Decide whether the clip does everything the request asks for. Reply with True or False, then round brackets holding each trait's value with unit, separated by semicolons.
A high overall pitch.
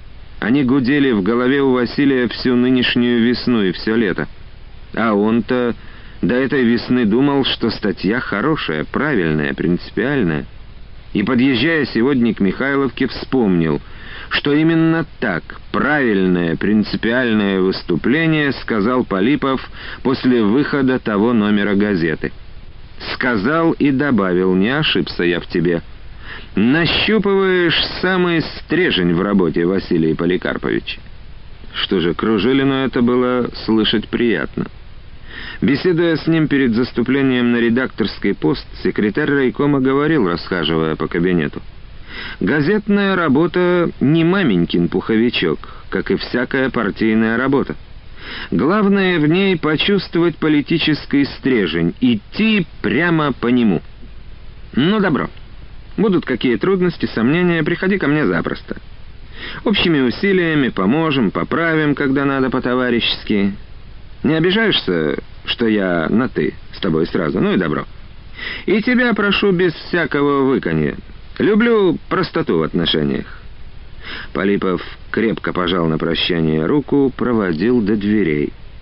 False (125 Hz)